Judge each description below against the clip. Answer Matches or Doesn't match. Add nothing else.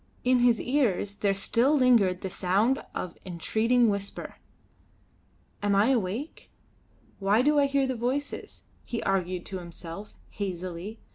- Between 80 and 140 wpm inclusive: Matches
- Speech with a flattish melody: Doesn't match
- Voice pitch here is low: Doesn't match